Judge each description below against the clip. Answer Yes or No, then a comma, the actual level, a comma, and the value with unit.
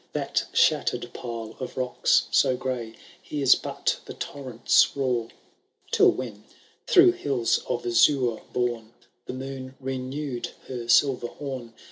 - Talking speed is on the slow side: Yes, slow, 125 wpm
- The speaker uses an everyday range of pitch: No, narrow, 2.1 semitones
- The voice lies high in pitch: No, low, 125 Hz